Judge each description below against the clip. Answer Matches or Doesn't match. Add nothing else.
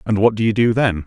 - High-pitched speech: Doesn't match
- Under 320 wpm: Doesn't match